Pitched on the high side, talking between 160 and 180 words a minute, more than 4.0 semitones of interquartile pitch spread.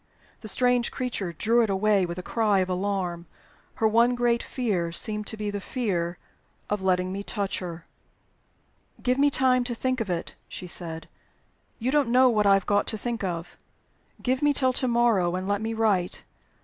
No: high, 210 Hz; average, 190 wpm; average, 4.7 semitones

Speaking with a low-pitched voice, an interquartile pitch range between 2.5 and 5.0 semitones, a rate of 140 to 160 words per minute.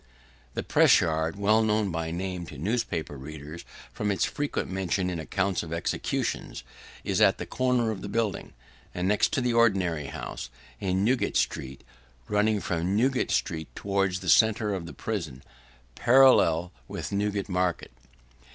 Yes: very low, 95 Hz; average, 4.3 semitones; average, 155 wpm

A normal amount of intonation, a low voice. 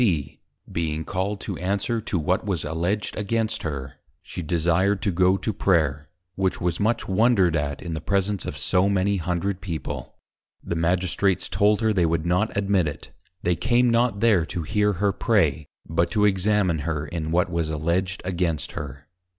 Yes: average, 3.6 semitones; very low, 90 Hz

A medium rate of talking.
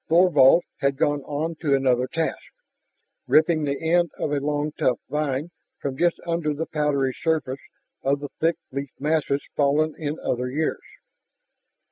Yes: average, 150 wpm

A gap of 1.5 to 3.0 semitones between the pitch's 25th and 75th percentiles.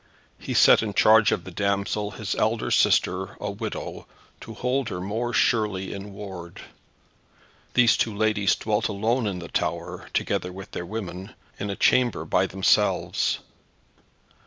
Yes: narrow, 2.5 semitones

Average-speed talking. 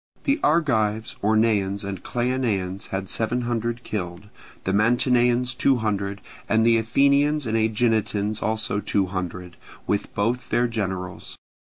No: slow, 130 wpm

